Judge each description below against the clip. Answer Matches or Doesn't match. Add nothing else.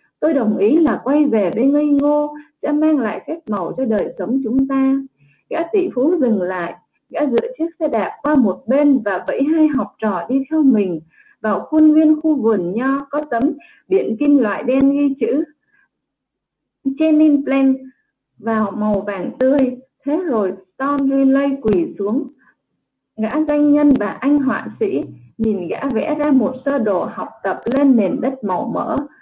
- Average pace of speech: Matches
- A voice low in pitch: Doesn't match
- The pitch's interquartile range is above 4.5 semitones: Matches